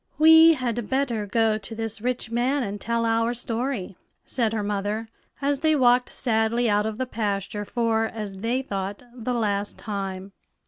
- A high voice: Yes, high, 225 Hz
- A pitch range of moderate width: Yes, average, 3.0 semitones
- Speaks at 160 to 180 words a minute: Yes, average, 170 wpm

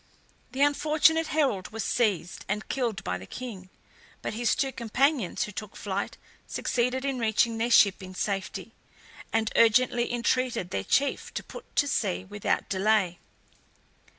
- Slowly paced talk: No, average, 150 wpm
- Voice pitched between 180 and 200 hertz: No, high, 225 Hz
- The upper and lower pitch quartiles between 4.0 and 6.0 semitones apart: Yes, average, 4.6 semitones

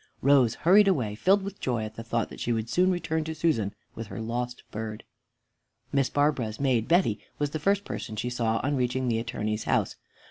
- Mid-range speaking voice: No, low, 125 Hz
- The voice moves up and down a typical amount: No, wide, 5.7 semitones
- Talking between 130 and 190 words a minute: No, fast, 205 wpm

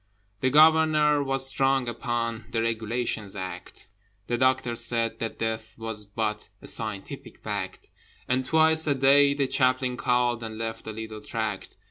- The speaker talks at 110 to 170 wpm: Yes, average, 150 wpm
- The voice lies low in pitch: Yes, low, 120 Hz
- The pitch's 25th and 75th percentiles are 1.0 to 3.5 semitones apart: Yes, average, 3.1 semitones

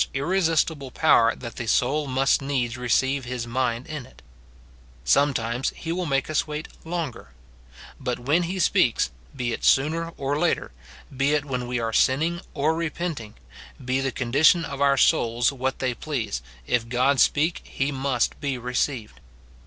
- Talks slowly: No, average, 165 wpm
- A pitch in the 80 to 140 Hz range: Yes, low, 135 Hz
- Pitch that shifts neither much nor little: Yes, average, 3.6 semitones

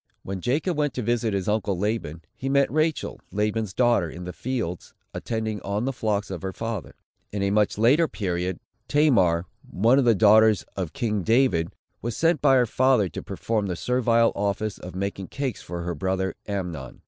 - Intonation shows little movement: No, average, 4.4 semitones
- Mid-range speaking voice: No, low, 105 Hz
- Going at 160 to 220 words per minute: Yes, average, 185 wpm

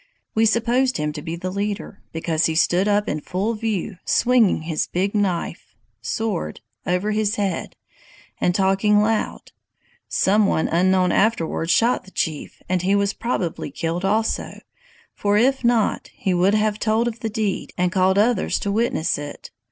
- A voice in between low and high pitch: No, high, 200 Hz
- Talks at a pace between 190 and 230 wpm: No, average, 165 wpm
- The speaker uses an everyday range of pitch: Yes, average, 3.6 semitones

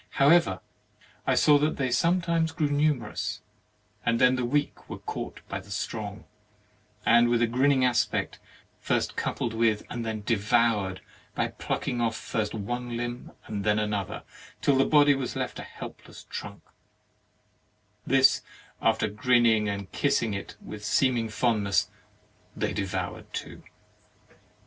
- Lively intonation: No, average, 4.1 semitones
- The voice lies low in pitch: Yes, low, 120 Hz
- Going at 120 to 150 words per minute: Yes, average, 140 wpm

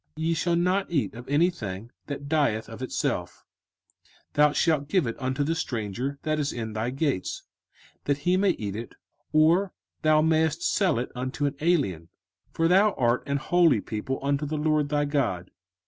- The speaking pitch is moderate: Yes, medium, 145 Hz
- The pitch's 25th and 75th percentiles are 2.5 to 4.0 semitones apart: No, average, 4.7 semitones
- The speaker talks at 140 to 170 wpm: No, average, 180 wpm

